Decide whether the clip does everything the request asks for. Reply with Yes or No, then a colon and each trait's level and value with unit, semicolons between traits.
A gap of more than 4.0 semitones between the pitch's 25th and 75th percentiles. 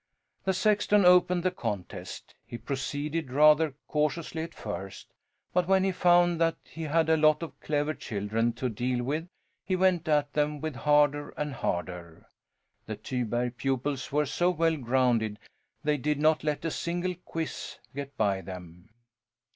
Yes: average, 5.0 semitones